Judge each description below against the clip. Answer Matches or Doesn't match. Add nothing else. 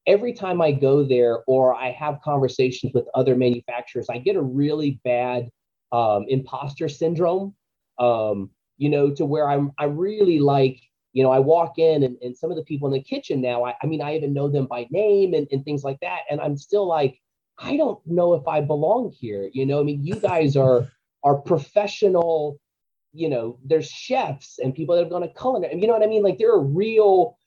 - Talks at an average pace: Doesn't match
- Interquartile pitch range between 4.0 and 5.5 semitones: Matches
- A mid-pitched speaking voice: Matches